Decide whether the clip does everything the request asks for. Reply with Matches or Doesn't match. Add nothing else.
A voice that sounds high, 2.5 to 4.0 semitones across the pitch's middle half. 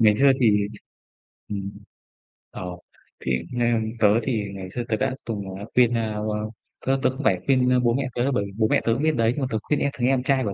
Doesn't match